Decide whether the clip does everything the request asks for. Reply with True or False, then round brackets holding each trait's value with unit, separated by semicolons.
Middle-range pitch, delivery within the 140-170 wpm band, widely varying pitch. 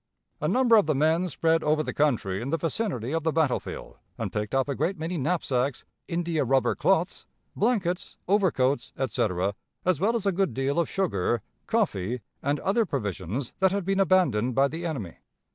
False (155 Hz; 180 wpm; 6.2 semitones)